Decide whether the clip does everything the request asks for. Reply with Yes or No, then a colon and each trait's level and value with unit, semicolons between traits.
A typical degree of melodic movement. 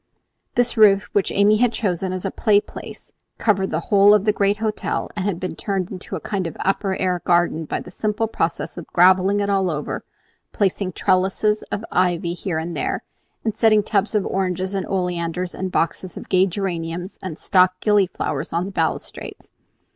No: narrow, 2.2 semitones